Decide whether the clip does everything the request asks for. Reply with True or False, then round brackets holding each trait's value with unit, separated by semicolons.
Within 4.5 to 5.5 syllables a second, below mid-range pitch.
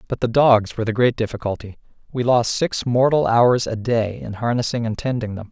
True (5.4 syllables/s; 115 Hz)